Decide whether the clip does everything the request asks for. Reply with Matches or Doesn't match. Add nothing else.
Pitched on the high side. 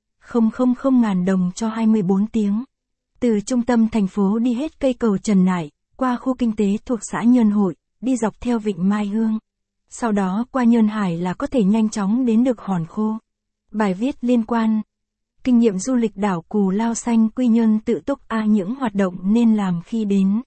Matches